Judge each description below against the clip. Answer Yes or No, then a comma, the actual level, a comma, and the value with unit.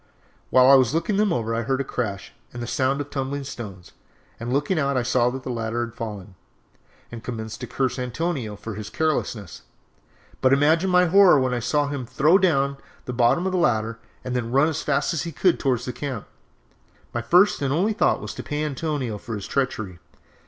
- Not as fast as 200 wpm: No, fast, 205 wpm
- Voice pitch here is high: No, low, 130 Hz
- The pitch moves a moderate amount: Yes, average, 4.3 semitones